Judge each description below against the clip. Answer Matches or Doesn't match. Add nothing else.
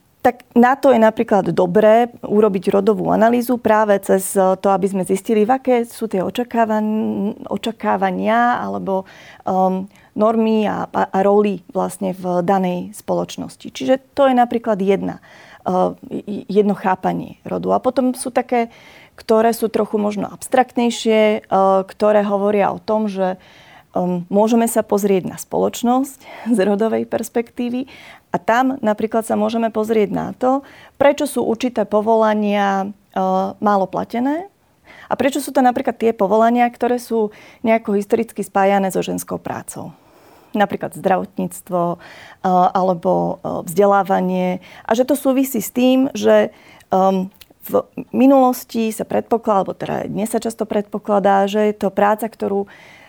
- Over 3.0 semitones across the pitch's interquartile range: Matches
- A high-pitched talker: Matches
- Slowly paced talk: Doesn't match